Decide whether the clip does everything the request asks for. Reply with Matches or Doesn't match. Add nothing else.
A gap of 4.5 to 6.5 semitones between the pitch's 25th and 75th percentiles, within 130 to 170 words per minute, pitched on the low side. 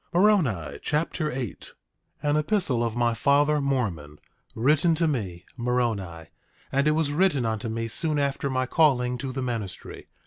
Matches